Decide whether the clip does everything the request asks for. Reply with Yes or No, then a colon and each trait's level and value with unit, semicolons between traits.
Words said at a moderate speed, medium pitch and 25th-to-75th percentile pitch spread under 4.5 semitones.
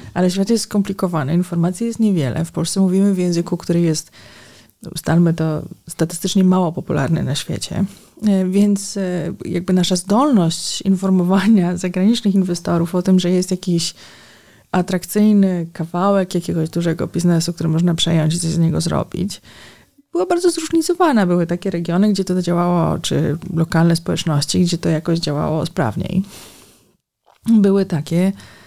Yes: average, 135 wpm; medium, 175 Hz; average, 2.8 semitones